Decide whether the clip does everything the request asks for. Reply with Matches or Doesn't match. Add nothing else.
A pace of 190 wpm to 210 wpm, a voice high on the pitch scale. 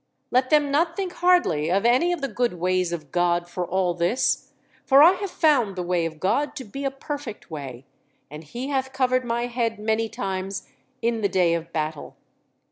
Matches